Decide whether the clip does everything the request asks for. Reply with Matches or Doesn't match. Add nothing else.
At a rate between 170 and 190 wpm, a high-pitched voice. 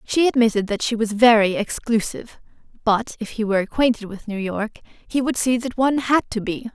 Doesn't match